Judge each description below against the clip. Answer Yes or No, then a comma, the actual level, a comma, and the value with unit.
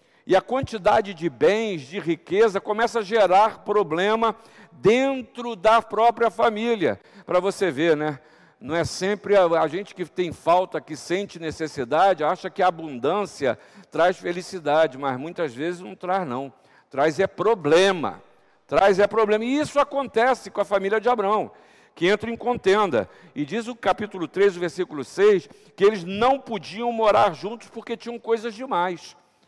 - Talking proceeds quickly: No, average, 160 wpm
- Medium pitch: No, high, 200 Hz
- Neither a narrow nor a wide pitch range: Yes, average, 4.3 semitones